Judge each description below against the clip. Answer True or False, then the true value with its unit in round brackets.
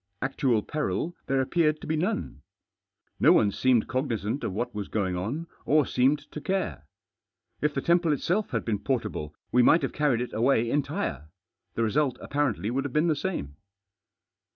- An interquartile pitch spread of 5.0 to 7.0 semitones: True (5.3 semitones)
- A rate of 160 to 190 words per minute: True (175 wpm)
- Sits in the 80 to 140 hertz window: True (135 Hz)